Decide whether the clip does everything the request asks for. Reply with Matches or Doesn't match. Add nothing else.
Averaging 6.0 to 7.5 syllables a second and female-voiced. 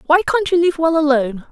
Matches